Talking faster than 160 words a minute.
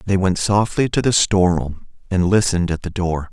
Yes: average, 200 wpm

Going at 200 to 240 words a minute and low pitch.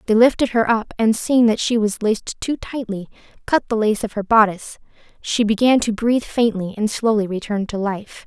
No: fast, 205 wpm; high, 220 Hz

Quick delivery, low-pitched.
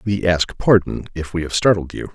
Yes: fast, 225 wpm; very low, 90 Hz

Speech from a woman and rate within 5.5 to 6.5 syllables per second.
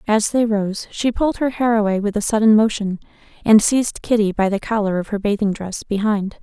Yes: female; 5.6 syllables/s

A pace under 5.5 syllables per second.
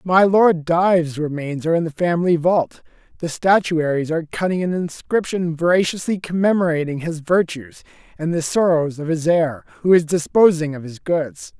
Yes: 5.0 syllables/s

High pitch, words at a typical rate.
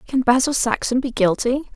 Yes: very high, 250 Hz; average, 170 wpm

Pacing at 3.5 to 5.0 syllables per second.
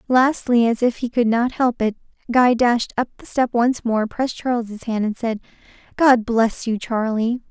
Yes: 4.5 syllables/s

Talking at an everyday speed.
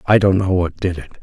No: fast, 295 wpm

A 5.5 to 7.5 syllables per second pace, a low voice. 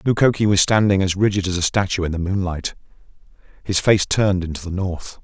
Yes: 6.0 syllables/s; very low, 95 Hz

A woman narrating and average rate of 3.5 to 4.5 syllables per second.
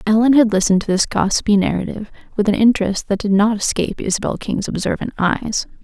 No: female; 6.4 syllables/s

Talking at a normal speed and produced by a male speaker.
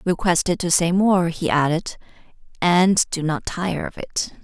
No: average, 165 wpm; female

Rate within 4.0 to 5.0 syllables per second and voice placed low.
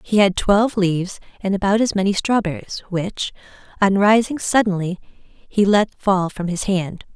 No: 4.5 syllables/s; high, 195 Hz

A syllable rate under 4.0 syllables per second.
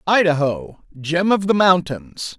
Yes: 3.7 syllables/s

